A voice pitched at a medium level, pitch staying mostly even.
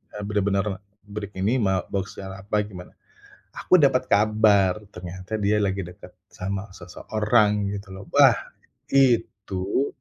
No: low, 100 Hz; narrow, 1.9 semitones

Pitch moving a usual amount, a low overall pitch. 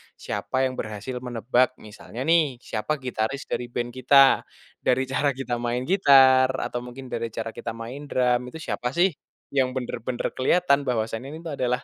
No: narrow, 2.0 semitones; low, 130 Hz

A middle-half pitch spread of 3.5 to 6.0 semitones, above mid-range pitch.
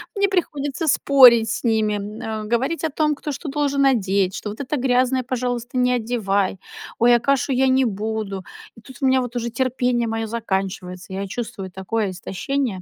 Yes: average, 3.9 semitones; high, 240 Hz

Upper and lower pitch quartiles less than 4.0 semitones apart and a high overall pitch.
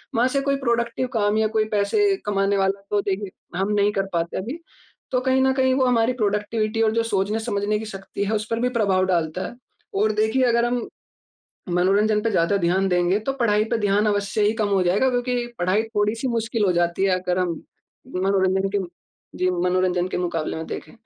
Yes: average, 3.3 semitones; high, 210 Hz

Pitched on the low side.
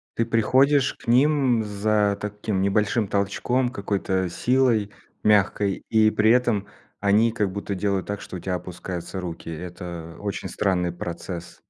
Yes: low, 100 Hz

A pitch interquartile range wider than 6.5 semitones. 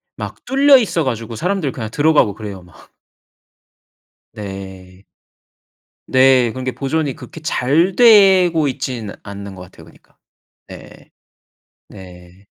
Yes: wide, 8.2 semitones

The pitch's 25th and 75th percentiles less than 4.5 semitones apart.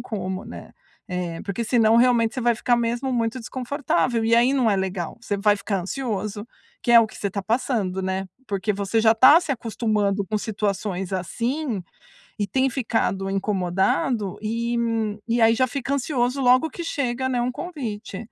Yes: average, 3.9 semitones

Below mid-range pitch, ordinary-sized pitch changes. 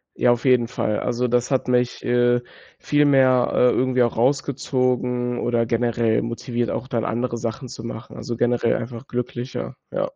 No: low, 120 Hz; narrow, 1.2 semitones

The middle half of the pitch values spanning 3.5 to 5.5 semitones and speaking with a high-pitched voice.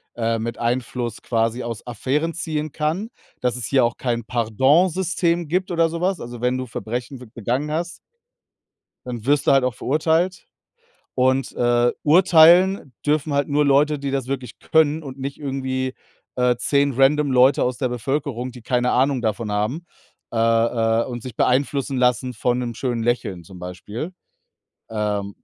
No: average, 3.9 semitones; low, 130 Hz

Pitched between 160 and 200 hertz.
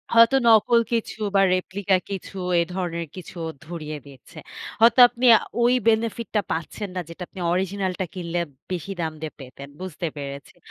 Yes: medium, 185 Hz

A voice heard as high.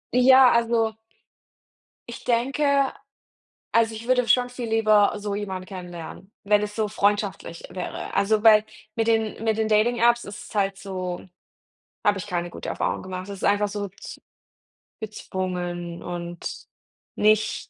Yes: high, 210 Hz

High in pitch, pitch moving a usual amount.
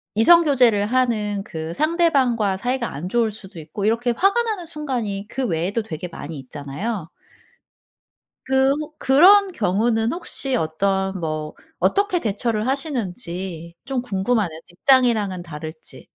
No: high, 220 Hz; wide, 6.7 semitones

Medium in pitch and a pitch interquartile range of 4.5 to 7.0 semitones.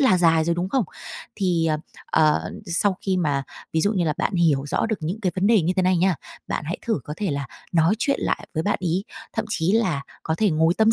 No: medium, 175 Hz; average, 4.0 semitones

